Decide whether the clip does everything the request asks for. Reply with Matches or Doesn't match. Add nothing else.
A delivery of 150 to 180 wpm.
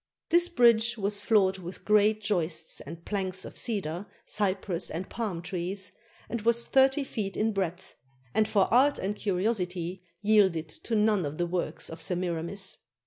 Matches